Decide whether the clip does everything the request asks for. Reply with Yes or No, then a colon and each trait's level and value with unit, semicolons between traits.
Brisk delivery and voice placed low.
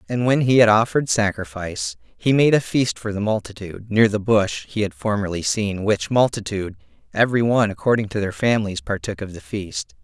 No: average, 190 wpm; low, 105 Hz